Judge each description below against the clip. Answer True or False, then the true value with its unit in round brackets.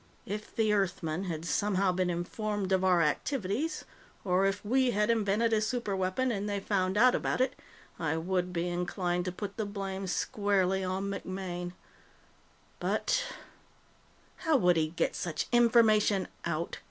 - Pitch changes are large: False (2.9 semitones)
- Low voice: False (195 Hz)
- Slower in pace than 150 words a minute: False (155 wpm)